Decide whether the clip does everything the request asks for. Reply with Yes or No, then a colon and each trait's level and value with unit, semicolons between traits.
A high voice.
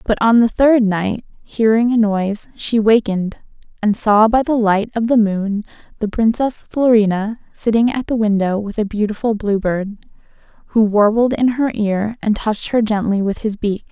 Yes: high, 215 Hz